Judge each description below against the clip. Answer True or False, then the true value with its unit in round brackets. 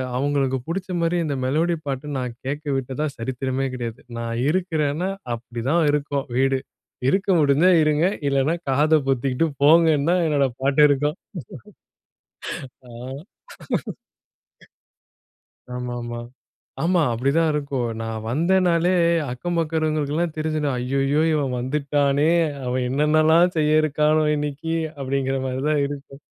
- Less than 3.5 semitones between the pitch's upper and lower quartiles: True (2.9 semitones)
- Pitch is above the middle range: False (145 Hz)